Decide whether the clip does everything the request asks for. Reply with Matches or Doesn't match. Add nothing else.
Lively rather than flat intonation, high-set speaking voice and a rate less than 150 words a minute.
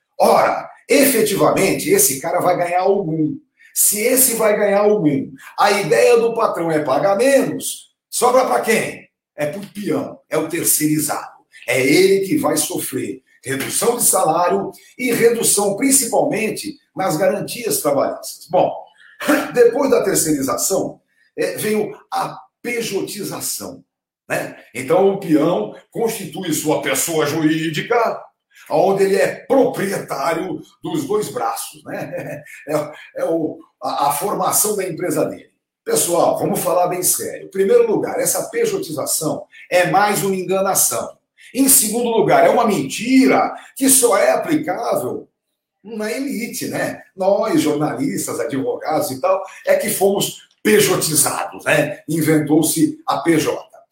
Matches